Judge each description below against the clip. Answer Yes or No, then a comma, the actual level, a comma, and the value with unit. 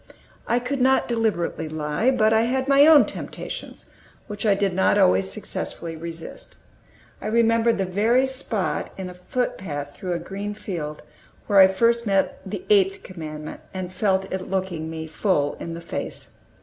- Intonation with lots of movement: Yes, wide, 5.7 semitones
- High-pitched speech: Yes, high, 195 Hz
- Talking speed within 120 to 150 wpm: No, average, 165 wpm